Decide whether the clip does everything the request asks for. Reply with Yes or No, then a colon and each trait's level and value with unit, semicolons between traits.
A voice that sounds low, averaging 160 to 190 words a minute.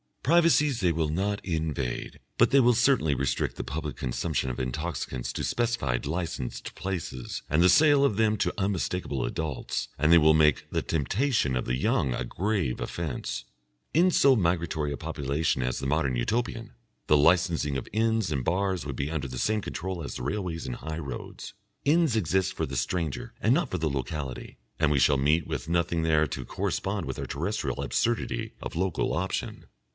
Yes: very low, 80 Hz; average, 185 wpm